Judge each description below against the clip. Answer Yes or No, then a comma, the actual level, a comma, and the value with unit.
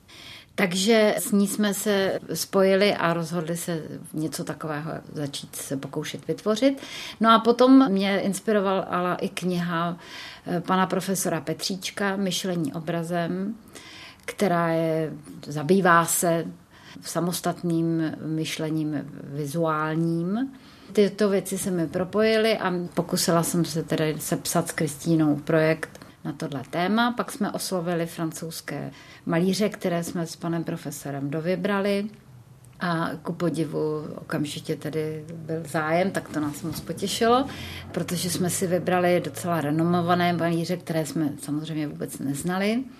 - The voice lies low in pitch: No, medium, 170 Hz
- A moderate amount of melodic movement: Yes, average, 3.2 semitones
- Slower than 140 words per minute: Yes, average, 120 wpm